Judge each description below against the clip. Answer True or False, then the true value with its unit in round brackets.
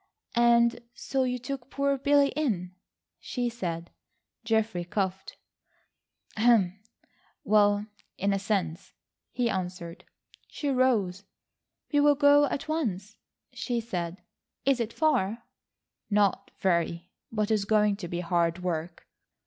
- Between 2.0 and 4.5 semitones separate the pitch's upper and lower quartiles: False (5.5 semitones)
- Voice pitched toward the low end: False (210 Hz)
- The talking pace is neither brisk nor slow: False (115 wpm)